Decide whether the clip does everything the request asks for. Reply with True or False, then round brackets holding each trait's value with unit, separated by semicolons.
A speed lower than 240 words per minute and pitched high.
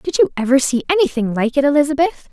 True (205 wpm; 280 Hz)